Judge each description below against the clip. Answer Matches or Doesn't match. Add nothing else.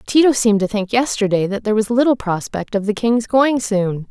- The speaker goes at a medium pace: Doesn't match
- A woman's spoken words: Matches